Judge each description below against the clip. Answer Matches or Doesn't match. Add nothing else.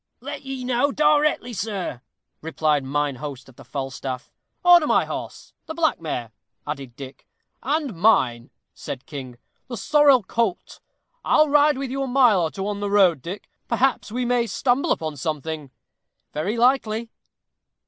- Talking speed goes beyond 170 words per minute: Doesn't match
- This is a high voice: Matches